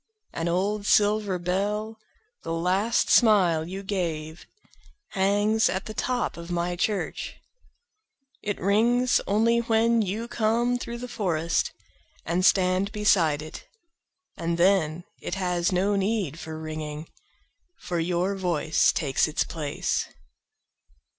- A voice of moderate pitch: No, high, 195 Hz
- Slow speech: Yes, slow, 110 wpm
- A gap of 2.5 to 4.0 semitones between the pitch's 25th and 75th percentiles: No, average, 4.5 semitones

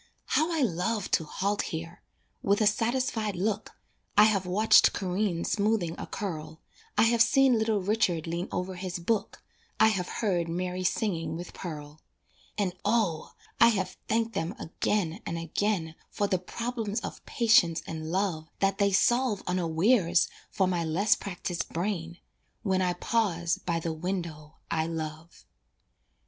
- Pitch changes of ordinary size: Yes, average, 4.1 semitones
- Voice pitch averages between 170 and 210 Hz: Yes, medium, 185 Hz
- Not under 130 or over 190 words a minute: Yes, average, 150 wpm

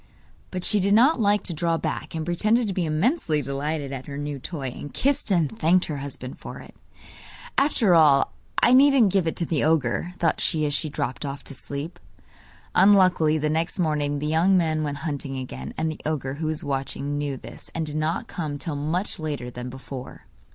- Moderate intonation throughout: Yes, average, 3.9 semitones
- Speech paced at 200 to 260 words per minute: Yes, fast, 205 wpm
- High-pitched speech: No, medium, 155 Hz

